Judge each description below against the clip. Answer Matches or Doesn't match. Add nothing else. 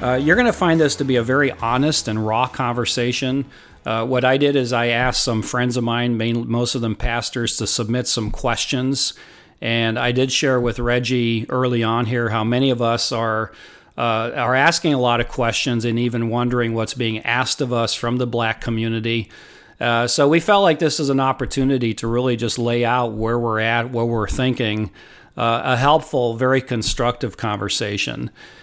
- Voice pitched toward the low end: Matches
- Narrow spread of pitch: Matches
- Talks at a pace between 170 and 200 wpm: Matches